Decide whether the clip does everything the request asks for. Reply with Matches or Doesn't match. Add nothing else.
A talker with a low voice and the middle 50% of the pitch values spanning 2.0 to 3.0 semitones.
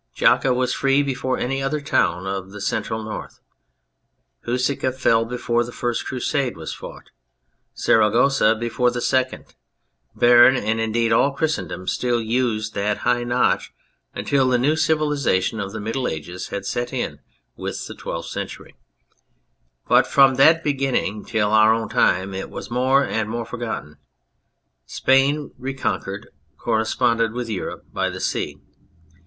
Doesn't match